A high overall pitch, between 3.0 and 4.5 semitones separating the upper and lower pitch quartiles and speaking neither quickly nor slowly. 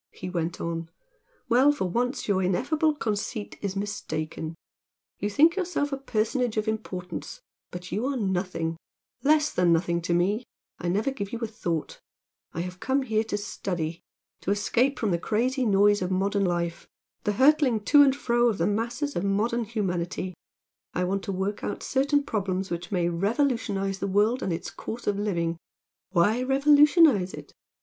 No: high, 205 Hz; wide, 5.6 semitones; average, 170 wpm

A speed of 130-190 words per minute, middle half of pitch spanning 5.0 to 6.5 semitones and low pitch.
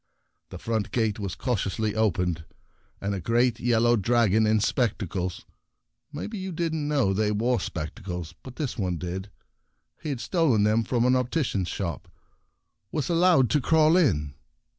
Yes: average, 160 wpm; average, 5.3 semitones; low, 115 Hz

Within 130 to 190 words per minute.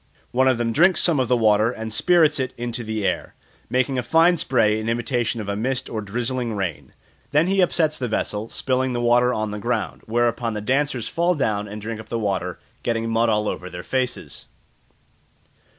No: average, 200 wpm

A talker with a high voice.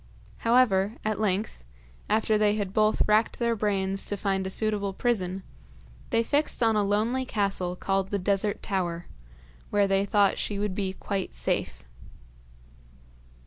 Yes: high, 205 Hz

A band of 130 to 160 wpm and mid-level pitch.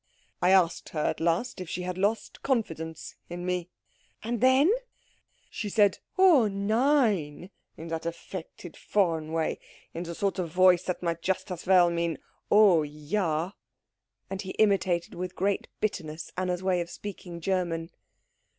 Yes: average, 150 wpm; medium, 180 Hz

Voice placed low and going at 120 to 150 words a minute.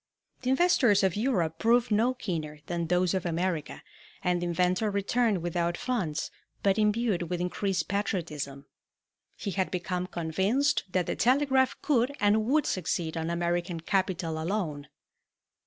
No: medium, 185 Hz; average, 140 wpm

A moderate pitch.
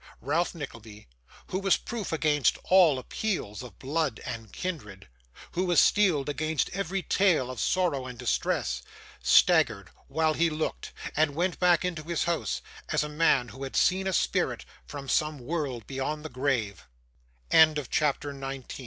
Yes: medium, 155 Hz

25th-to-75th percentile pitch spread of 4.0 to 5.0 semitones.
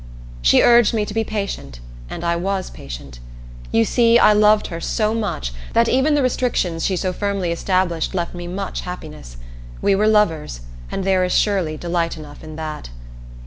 Yes: average, 4.4 semitones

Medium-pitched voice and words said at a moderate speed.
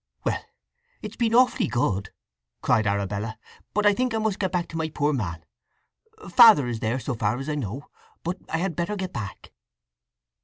Yes: medium, 150 Hz; average, 180 wpm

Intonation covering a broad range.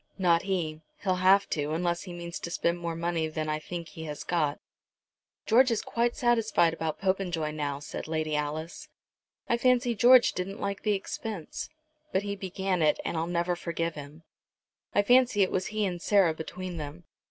No: average, 3.8 semitones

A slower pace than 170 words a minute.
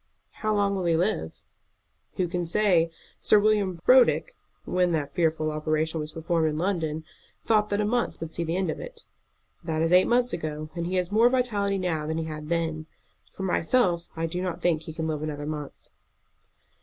No: average, 200 wpm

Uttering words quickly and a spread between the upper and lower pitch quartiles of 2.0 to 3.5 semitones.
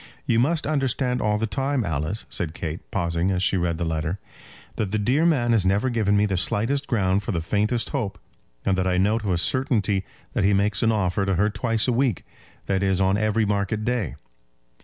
No: fast, 215 wpm; average, 3.9 semitones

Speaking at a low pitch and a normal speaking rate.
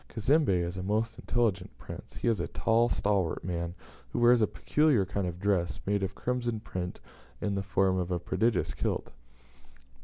Yes: low, 100 Hz; average, 180 wpm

